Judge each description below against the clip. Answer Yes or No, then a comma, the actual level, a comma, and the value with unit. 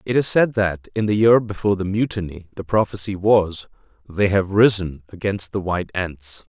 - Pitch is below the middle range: Yes, low, 100 Hz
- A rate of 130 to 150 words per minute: No, average, 185 wpm